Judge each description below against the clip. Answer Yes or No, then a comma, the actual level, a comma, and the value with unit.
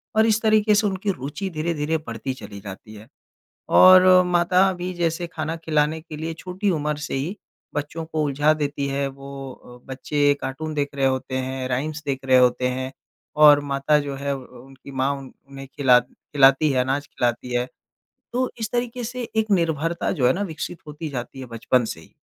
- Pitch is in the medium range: Yes, medium, 145 Hz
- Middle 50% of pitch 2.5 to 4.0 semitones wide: No, average, 4.5 semitones